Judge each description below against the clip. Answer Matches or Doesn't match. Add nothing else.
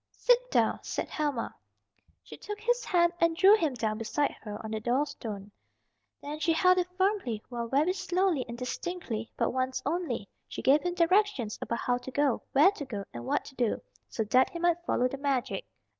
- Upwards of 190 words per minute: Matches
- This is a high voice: Matches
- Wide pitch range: Matches